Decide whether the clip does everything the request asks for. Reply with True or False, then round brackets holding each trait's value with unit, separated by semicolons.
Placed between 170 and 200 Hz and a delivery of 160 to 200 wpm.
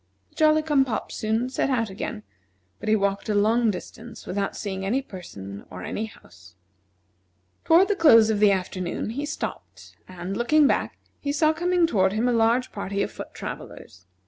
False (220 Hz; 180 wpm)